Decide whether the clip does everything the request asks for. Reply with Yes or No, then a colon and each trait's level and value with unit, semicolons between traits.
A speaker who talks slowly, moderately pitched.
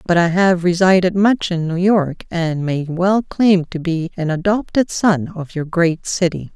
No: average, 190 wpm; medium, 175 Hz